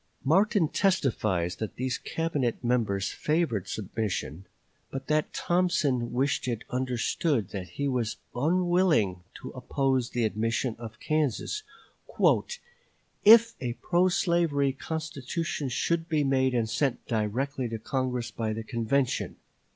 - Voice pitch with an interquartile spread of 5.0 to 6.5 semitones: Yes, wide, 5.5 semitones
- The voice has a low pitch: Yes, low, 130 Hz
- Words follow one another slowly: Yes, slow, 120 wpm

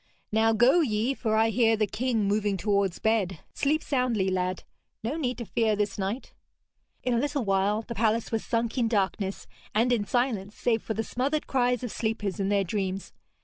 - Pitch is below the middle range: No, high, 220 Hz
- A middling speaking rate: Yes, average, 190 wpm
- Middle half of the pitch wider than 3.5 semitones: No, average, 3.2 semitones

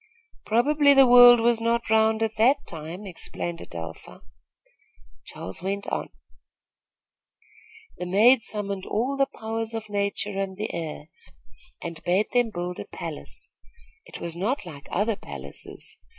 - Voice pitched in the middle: No, high, 210 Hz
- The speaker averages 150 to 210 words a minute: No, slow, 135 wpm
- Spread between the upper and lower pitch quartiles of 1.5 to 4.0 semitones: No, average, 4.7 semitones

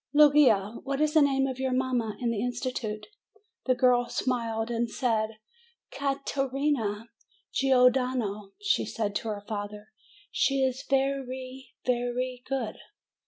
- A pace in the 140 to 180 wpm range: Yes, average, 160 wpm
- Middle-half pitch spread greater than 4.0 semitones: No, average, 3.2 semitones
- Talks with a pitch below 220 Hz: No, very high, 250 Hz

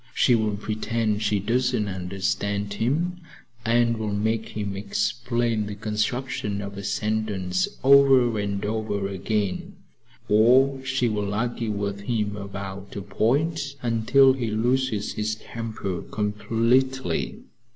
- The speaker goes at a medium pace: No, slow, 120 wpm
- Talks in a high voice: No, low, 110 Hz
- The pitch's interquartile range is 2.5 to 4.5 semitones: Yes, average, 2.9 semitones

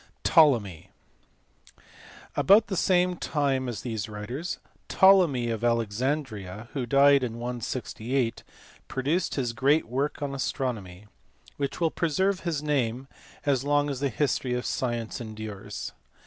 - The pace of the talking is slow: Yes, slow, 125 wpm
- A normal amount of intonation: Yes, average, 4.1 semitones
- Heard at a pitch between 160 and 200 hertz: No, low, 130 Hz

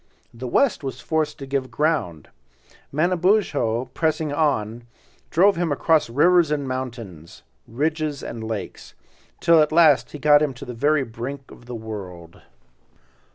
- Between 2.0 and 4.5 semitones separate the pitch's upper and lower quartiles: No, average, 5.1 semitones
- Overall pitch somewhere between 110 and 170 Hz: Yes, medium, 140 Hz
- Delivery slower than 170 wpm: Yes, average, 145 wpm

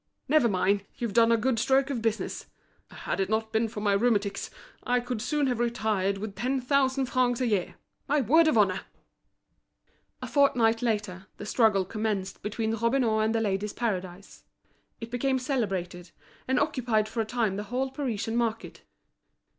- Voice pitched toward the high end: Yes, high, 225 Hz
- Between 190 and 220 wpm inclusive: No, average, 170 wpm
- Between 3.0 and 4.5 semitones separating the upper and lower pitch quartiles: Yes, average, 3.3 semitones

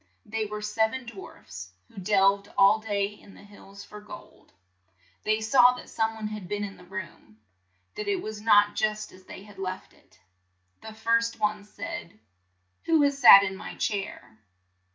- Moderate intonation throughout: No, narrow, 2.0 semitones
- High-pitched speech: Yes, high, 210 Hz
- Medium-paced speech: Yes, average, 175 wpm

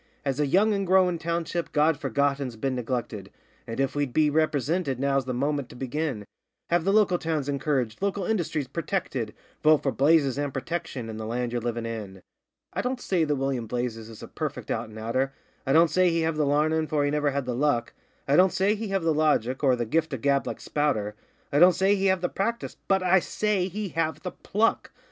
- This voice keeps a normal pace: No, fast, 220 wpm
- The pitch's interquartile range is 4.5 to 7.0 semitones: Yes, average, 5.1 semitones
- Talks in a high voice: No, medium, 145 Hz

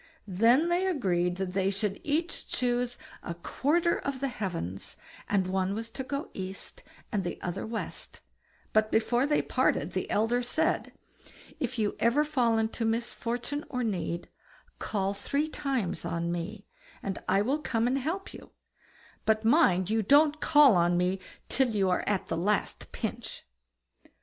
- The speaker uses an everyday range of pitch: No, wide, 6.1 semitones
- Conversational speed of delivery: Yes, average, 160 wpm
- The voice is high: Yes, high, 225 Hz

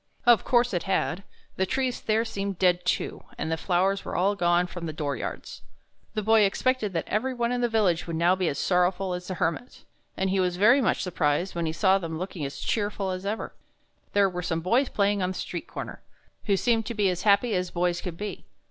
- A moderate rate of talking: No, fast, 230 wpm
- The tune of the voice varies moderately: Yes, average, 3.2 semitones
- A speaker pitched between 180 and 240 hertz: Yes, high, 190 Hz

